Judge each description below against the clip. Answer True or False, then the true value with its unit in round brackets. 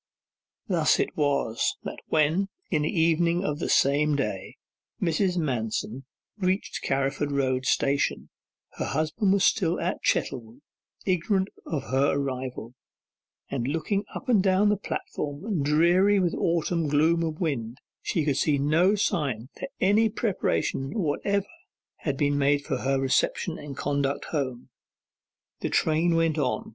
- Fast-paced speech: False (145 wpm)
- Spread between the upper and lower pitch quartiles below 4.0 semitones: False (4.6 semitones)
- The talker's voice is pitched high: False (155 Hz)